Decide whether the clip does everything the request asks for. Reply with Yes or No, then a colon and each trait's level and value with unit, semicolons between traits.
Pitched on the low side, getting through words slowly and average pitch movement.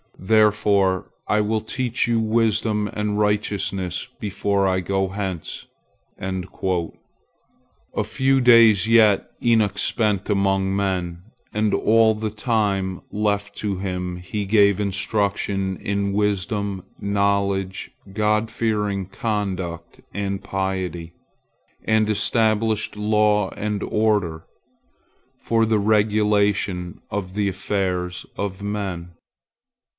No: low, 100 Hz; slow, 100 wpm; narrow, 1.9 semitones